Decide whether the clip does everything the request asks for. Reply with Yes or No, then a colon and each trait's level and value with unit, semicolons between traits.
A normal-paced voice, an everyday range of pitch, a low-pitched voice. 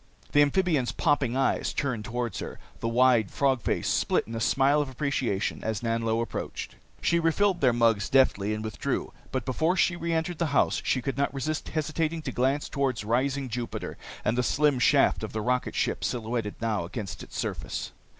Yes: average, 180 wpm; average, 4.2 semitones; low, 130 Hz